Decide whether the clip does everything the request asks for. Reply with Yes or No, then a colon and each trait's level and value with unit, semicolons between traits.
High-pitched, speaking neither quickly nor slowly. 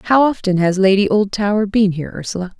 Yes: high, 200 Hz; average, 185 wpm